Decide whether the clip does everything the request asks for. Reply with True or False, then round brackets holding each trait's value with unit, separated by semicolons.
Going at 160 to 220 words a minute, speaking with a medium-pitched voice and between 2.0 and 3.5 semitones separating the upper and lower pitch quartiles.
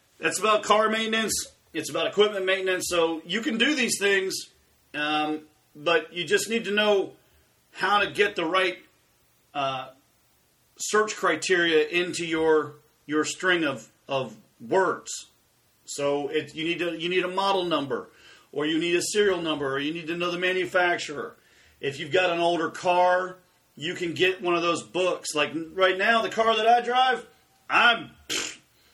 False (170 wpm; 175 Hz; 4.2 semitones)